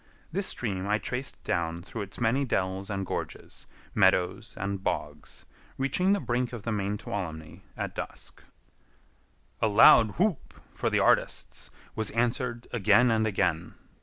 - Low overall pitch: Yes, low, 110 Hz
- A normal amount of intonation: Yes, average, 3.9 semitones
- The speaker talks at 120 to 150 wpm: Yes, average, 145 wpm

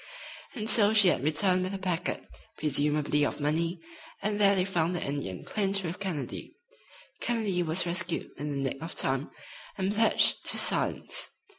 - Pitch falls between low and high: Yes, medium, 175 Hz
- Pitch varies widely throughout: No, average, 4.8 semitones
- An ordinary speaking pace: Yes, average, 165 wpm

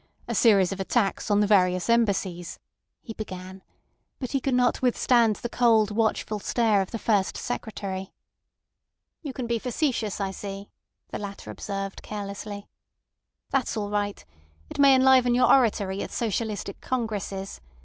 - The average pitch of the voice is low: No, high, 210 Hz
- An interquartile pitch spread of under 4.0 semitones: Yes, average, 3.3 semitones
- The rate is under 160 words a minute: Yes, average, 150 wpm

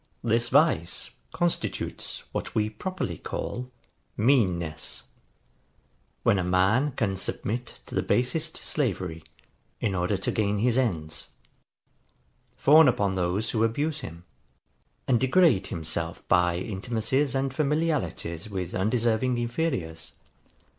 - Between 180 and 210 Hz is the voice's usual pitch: No, low, 110 Hz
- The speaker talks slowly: Yes, slow, 115 wpm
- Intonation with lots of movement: Yes, wide, 6.3 semitones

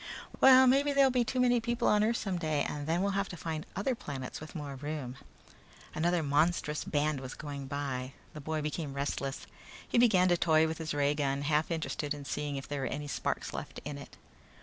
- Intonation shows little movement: No, average, 4.5 semitones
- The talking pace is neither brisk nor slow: No, fast, 215 wpm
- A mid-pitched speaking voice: Yes, medium, 155 Hz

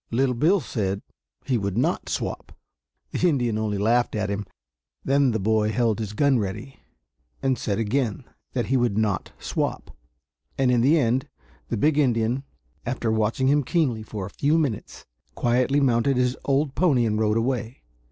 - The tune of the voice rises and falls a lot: No, average, 3.7 semitones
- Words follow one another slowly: No, average, 170 wpm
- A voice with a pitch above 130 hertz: No, low, 120 Hz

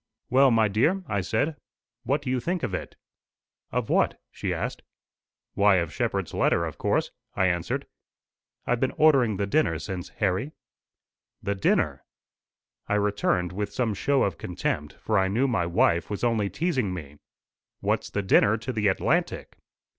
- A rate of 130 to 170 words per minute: Yes, average, 160 wpm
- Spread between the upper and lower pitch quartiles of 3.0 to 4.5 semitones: No, wide, 5.5 semitones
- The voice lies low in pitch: Yes, low, 105 Hz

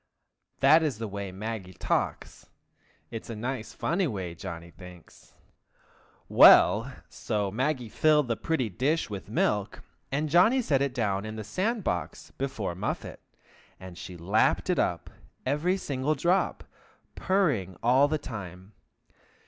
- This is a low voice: Yes, low, 115 Hz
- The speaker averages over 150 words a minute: No, average, 140 wpm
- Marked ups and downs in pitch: Yes, wide, 7.2 semitones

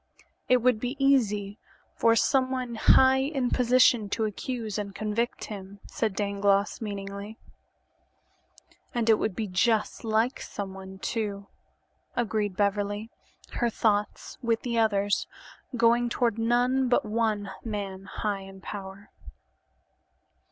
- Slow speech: Yes, slow, 120 wpm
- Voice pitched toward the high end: Yes, high, 215 Hz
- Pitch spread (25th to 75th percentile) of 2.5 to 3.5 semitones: Yes, average, 2.9 semitones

